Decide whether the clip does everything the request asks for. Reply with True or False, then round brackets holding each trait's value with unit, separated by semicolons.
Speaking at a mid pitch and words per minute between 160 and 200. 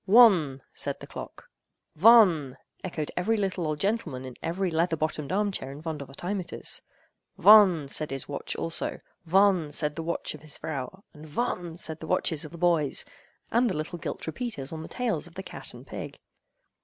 True (165 Hz; 180 wpm)